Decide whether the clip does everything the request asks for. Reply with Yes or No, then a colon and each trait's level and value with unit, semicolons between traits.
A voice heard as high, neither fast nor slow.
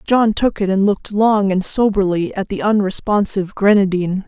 Yes: high, 200 Hz; average, 170 wpm